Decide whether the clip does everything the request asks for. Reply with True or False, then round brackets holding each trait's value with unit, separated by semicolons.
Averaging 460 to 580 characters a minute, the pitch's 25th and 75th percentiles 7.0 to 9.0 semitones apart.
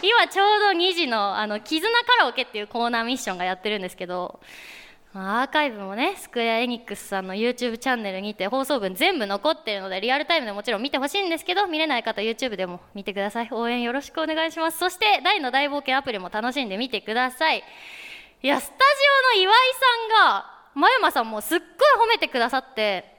True (475 characters per minute; 7.9 semitones)